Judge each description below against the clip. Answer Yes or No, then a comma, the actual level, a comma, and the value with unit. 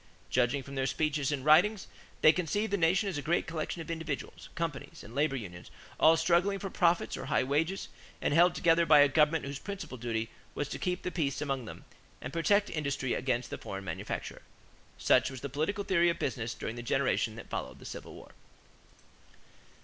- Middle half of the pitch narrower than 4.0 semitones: No, average, 4.3 semitones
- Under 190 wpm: No, average, 195 wpm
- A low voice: No, medium, 150 Hz